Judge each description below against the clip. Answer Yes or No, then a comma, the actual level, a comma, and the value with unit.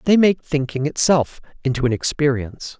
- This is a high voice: No, medium, 145 Hz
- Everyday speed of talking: Yes, average, 150 wpm